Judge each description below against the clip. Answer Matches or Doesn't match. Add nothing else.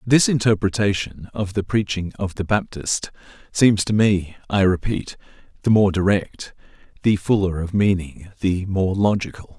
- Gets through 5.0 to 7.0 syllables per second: Doesn't match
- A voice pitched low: Matches